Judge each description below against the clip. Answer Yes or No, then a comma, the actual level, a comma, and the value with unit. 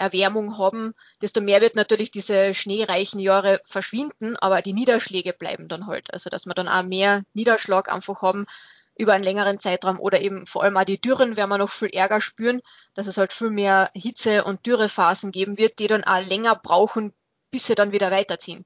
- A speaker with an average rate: No, fast, 200 wpm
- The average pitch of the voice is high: Yes, high, 200 Hz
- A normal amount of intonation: No, narrow, 2.3 semitones